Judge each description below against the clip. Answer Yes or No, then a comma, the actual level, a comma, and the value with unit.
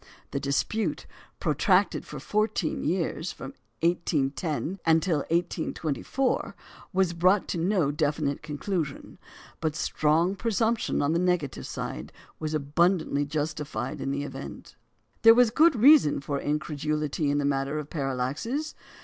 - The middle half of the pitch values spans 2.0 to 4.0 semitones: No, average, 4.5 semitones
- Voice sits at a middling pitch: Yes, medium, 155 Hz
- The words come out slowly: Yes, slow, 130 wpm